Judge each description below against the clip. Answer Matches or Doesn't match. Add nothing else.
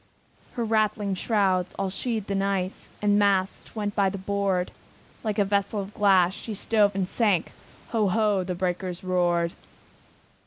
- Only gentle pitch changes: Matches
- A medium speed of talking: Matches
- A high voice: Matches